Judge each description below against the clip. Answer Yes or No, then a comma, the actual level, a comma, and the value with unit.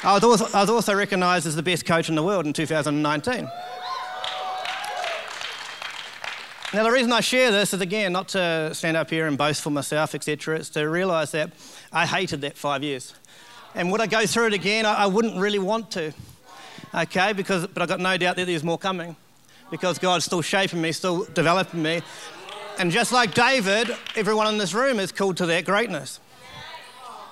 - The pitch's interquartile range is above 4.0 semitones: Yes, average, 4.7 semitones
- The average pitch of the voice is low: No, medium, 185 Hz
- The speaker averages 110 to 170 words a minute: No, average, 185 wpm